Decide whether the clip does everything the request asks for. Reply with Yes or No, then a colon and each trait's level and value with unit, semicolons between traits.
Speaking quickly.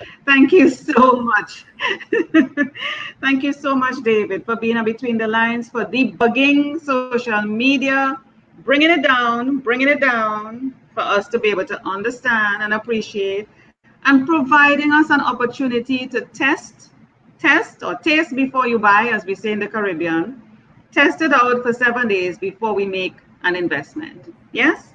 No: average, 155 wpm